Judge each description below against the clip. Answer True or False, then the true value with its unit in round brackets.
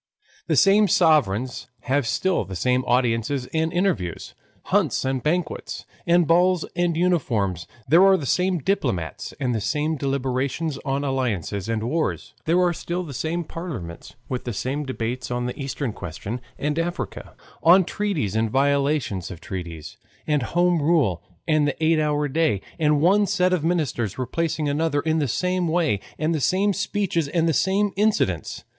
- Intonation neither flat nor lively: False (5.7 semitones)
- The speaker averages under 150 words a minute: False (165 wpm)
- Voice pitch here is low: False (150 Hz)